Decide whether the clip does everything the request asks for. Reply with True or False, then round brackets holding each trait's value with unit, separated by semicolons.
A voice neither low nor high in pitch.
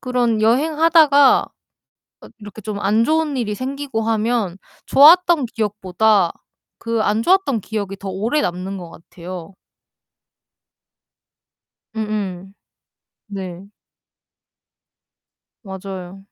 False (215 Hz)